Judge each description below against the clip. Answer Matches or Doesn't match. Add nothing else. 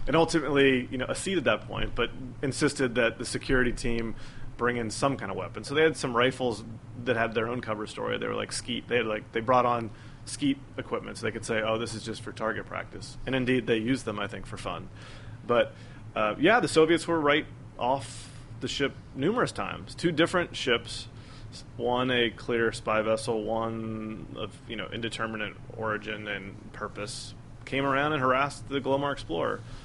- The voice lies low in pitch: Matches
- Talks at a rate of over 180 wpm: Matches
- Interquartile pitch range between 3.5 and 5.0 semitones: Doesn't match